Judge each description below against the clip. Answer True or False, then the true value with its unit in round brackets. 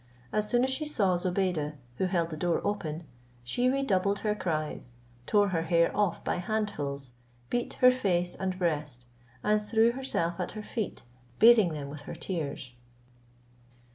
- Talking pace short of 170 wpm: True (160 wpm)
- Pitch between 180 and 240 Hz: True (185 Hz)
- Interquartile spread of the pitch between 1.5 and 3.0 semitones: False (4.6 semitones)